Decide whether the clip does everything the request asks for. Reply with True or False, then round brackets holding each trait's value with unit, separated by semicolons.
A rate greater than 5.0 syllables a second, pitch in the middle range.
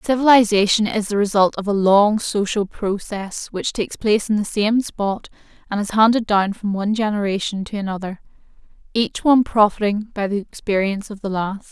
False (5.4 syllables/s; 210 Hz)